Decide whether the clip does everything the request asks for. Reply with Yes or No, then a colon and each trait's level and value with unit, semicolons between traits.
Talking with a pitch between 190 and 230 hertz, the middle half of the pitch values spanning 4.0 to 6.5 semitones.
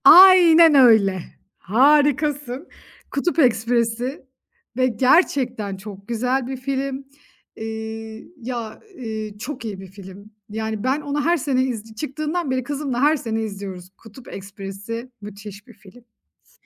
No: high, 240 Hz; average, 4.5 semitones